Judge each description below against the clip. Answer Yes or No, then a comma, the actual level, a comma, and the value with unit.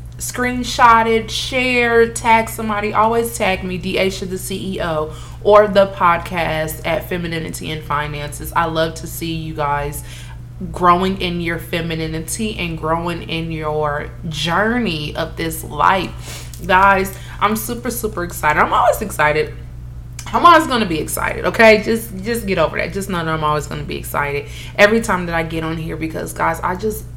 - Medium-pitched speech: Yes, medium, 165 Hz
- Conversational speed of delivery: Yes, average, 165 wpm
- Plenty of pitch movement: No, average, 4.7 semitones